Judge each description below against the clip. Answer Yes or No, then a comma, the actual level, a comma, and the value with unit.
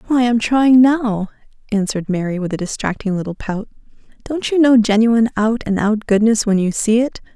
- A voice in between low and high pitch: No, high, 220 Hz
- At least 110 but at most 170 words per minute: No, average, 190 wpm